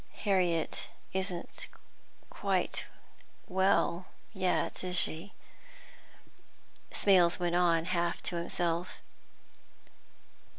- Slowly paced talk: Yes, slow, 75 wpm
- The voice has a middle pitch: Yes, medium, 175 Hz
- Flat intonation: Yes, narrow, 1.6 semitones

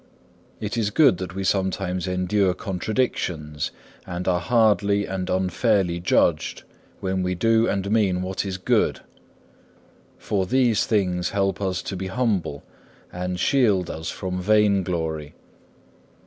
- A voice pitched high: No, very low, 95 Hz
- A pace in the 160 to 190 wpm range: No, slow, 135 wpm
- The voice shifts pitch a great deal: No, narrow, 2.4 semitones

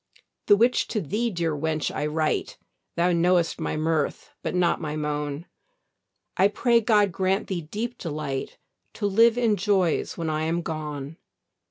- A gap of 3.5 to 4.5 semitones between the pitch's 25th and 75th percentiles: No, average, 4.9 semitones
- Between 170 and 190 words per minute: No, average, 160 wpm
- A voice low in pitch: No, medium, 170 Hz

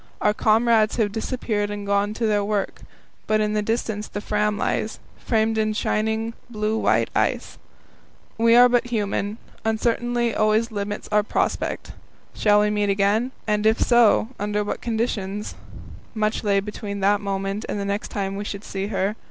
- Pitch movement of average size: No, narrow, 1.4 semitones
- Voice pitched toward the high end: Yes, high, 210 Hz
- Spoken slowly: No, average, 170 wpm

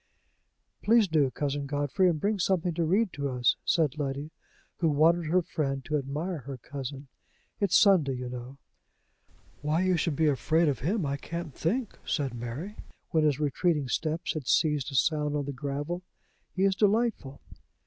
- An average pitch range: Yes, average, 3.9 semitones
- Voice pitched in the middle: Yes, medium, 150 Hz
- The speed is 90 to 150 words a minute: No, average, 170 wpm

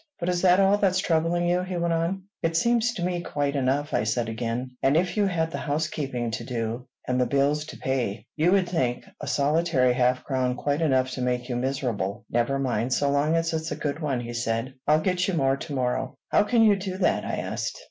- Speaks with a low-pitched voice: No, medium, 145 Hz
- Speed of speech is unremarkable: No, fast, 230 wpm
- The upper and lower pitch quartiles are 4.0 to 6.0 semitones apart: Yes, wide, 5.5 semitones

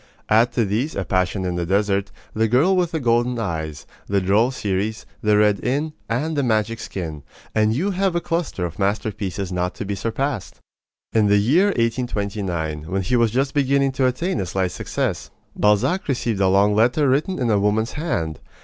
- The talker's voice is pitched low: Yes, low, 110 Hz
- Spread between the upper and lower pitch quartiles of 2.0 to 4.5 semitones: No, average, 5.1 semitones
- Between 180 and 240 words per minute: Yes, average, 190 wpm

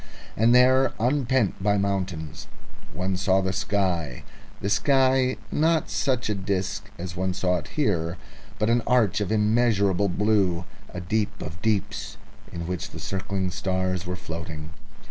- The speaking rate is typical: Yes, average, 145 wpm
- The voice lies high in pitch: No, low, 100 Hz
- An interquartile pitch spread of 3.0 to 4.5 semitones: Yes, average, 3.5 semitones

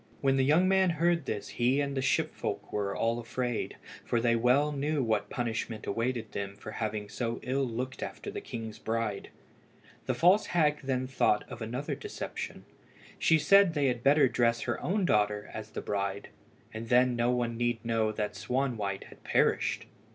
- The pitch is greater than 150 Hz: No, low, 120 Hz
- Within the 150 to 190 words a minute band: Yes, average, 180 wpm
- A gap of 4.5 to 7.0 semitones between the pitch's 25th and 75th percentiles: No, average, 3.9 semitones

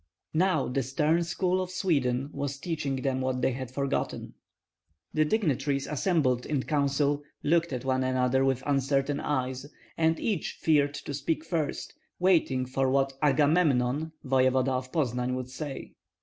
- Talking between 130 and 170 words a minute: Yes, average, 150 wpm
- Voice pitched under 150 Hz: Yes, medium, 140 Hz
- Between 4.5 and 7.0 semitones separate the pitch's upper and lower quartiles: No, average, 3.1 semitones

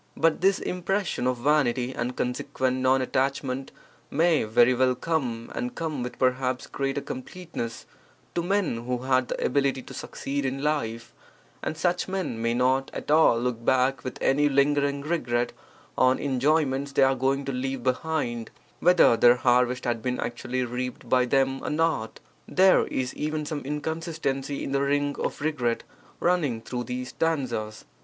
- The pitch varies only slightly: No, average, 3.1 semitones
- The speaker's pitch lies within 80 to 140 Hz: Yes, low, 135 Hz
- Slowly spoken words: No, average, 160 wpm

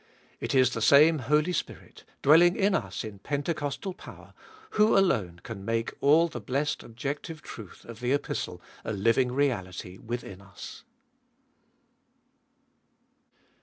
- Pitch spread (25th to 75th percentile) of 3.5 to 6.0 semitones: Yes, average, 5.2 semitones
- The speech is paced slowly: Yes, slow, 130 wpm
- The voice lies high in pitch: No, low, 130 Hz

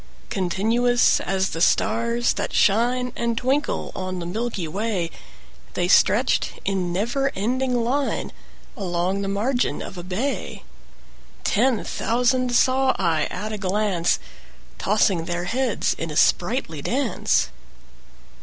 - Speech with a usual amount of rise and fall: Yes, average, 5.0 semitones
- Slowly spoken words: Yes, slow, 125 wpm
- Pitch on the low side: No, high, 215 Hz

